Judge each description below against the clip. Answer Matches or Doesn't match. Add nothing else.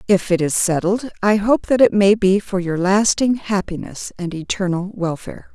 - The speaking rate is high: Doesn't match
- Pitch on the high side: Matches